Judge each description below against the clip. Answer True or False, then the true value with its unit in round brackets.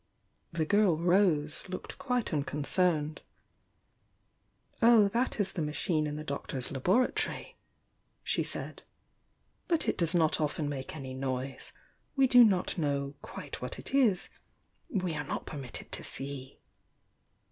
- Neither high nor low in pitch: True (155 Hz)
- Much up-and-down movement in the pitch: True (5.8 semitones)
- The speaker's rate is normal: True (145 wpm)